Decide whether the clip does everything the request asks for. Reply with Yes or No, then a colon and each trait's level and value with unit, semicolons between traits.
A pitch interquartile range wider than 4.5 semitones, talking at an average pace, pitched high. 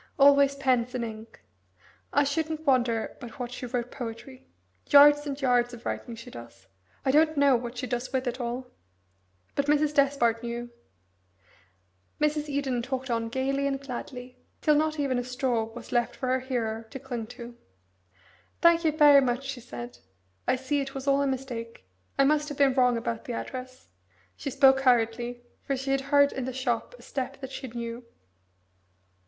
No: average, 2.7 semitones; average, 180 wpm; very high, 260 Hz